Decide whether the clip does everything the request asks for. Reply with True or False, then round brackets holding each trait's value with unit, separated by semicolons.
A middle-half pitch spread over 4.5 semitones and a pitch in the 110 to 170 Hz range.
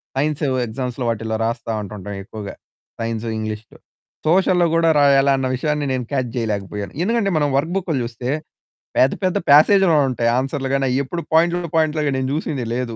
True (5.0 semitones; 135 Hz)